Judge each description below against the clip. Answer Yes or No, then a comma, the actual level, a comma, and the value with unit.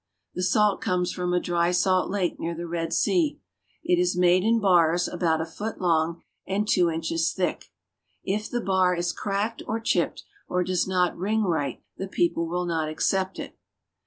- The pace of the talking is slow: No, average, 185 wpm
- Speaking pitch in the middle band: Yes, medium, 180 Hz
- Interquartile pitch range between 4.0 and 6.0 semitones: No, narrow, 2.4 semitones